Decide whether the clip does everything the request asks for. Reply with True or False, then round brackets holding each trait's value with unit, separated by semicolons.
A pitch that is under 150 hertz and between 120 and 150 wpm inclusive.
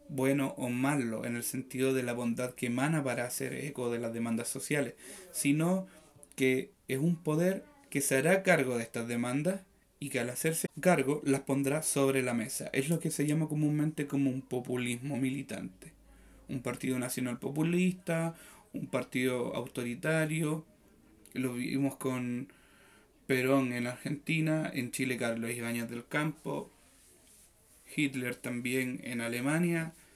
True (135 Hz; 145 wpm)